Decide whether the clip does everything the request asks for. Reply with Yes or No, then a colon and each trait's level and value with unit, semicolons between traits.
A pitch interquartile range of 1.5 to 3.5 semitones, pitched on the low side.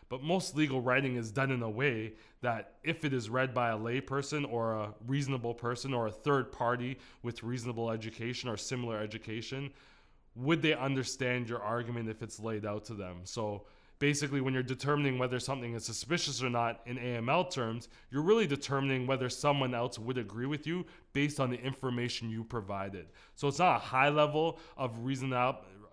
Yes: average, 3.1 semitones; low, 125 Hz